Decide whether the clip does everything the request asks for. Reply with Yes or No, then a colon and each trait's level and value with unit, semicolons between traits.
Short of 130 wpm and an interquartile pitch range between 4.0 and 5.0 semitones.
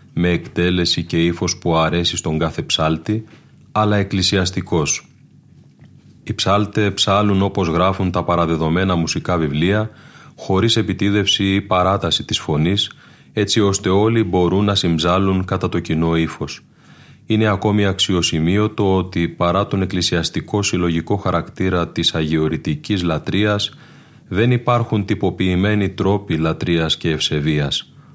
No: average, 120 wpm; average, 3.4 semitones